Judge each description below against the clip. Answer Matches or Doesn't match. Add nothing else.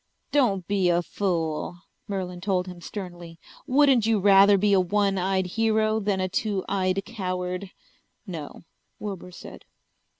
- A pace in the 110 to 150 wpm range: Matches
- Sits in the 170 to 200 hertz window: Matches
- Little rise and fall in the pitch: Matches